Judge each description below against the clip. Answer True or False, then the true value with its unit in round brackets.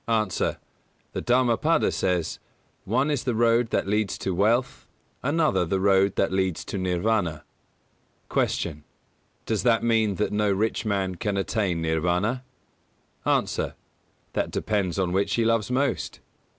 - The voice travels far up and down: False (3.7 semitones)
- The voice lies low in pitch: True (105 Hz)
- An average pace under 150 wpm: True (140 wpm)